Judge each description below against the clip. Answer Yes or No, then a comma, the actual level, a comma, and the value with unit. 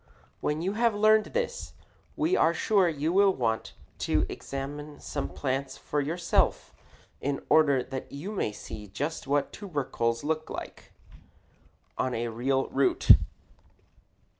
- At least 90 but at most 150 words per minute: Yes, slow, 135 wpm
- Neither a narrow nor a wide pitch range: No, wide, 5.8 semitones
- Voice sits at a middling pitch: Yes, medium, 145 Hz